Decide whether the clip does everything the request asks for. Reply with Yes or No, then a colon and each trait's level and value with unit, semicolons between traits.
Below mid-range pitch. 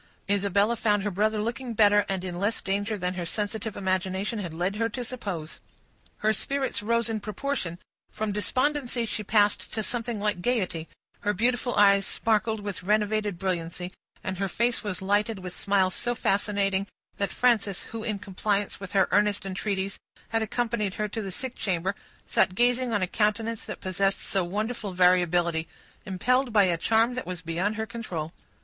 No: high, 205 Hz